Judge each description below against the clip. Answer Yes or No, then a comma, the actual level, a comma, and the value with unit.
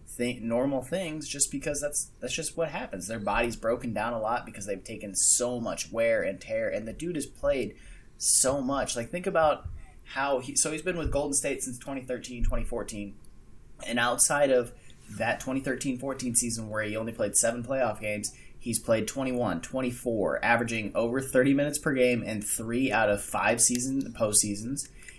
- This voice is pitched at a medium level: No, low, 125 Hz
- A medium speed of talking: Yes, average, 180 wpm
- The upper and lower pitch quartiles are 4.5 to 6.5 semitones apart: No, average, 3.5 semitones